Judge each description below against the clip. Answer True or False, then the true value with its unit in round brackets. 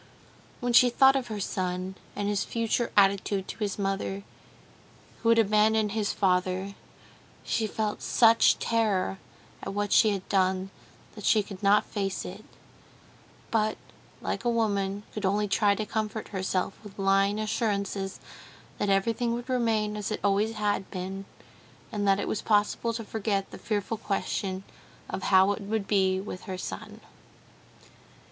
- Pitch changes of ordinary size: False (2.1 semitones)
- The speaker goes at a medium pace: True (155 wpm)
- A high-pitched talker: True (205 Hz)